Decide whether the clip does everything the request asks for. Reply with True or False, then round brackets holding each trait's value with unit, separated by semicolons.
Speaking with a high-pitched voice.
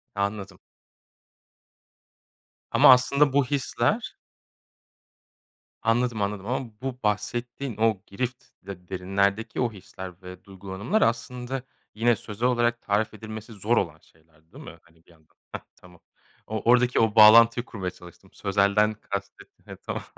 False (110 Hz)